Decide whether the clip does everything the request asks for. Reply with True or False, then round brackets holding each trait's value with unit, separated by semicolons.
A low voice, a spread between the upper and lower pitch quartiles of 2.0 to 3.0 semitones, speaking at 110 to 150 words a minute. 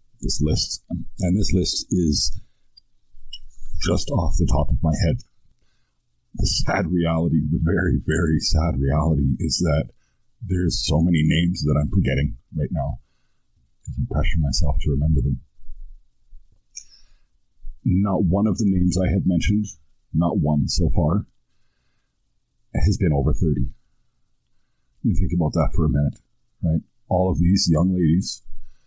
False (85 Hz; 3.6 semitones; 140 wpm)